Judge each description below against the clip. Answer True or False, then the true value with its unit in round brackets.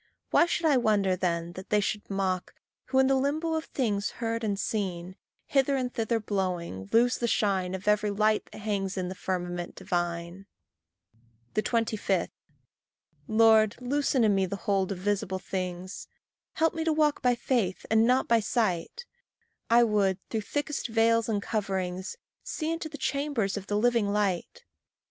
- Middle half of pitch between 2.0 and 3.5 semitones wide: False (4.4 semitones)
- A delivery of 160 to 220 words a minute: True (165 wpm)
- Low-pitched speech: False (210 Hz)